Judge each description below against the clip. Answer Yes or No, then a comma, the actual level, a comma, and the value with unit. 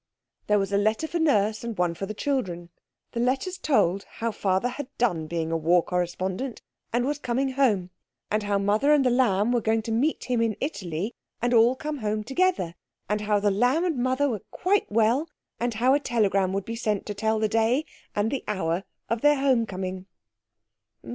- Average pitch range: Yes, average, 4.7 semitones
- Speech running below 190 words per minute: No, average, 200 wpm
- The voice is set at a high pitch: Yes, high, 220 Hz